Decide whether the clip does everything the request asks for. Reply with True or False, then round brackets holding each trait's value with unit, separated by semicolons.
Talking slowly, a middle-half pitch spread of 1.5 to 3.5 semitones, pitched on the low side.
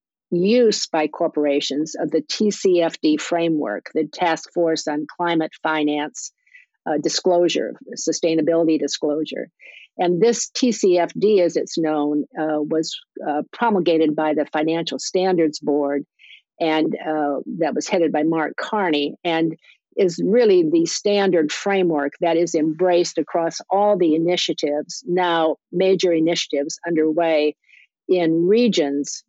False (120 wpm; 2.7 semitones; 165 Hz)